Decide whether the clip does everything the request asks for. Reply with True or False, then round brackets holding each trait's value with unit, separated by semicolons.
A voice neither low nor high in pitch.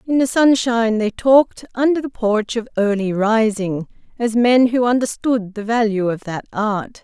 False (225 Hz)